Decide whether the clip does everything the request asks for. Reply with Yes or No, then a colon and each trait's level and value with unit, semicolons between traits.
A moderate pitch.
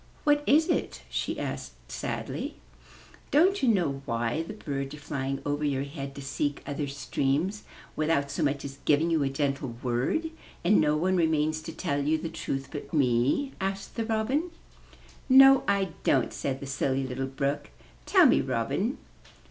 Yes: medium, 145 Hz